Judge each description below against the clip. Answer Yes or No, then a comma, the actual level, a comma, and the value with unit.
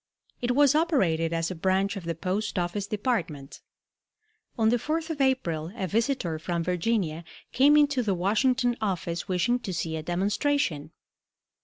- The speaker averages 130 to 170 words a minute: Yes, average, 155 wpm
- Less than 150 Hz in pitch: No, high, 200 Hz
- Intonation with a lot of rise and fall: Yes, wide, 6.7 semitones